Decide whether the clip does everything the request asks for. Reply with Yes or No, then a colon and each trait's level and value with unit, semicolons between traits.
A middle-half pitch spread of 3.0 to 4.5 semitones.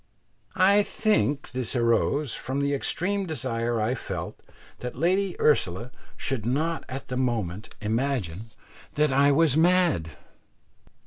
No: wide, 5.4 semitones